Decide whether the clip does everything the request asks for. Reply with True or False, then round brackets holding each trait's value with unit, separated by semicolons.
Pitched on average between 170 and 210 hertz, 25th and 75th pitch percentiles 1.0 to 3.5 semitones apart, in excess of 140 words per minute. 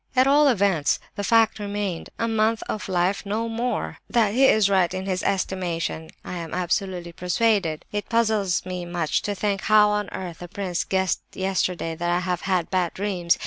True (190 Hz; 3.2 semitones; 185 wpm)